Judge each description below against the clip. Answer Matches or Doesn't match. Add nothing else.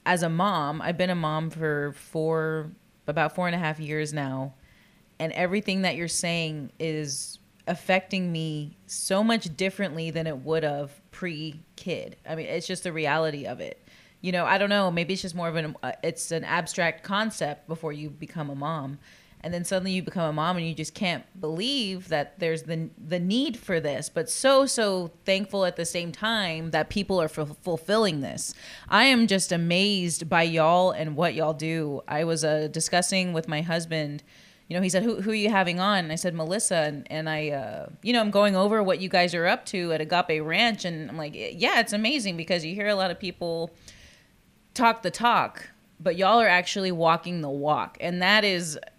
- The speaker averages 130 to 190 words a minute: Doesn't match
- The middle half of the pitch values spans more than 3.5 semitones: Doesn't match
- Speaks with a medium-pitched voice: Matches